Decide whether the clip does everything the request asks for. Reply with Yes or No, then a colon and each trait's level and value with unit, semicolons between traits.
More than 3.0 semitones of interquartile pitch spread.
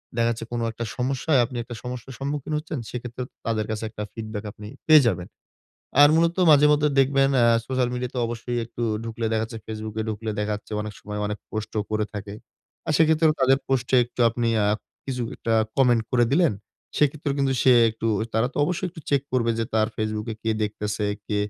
Yes: average, 3.8 semitones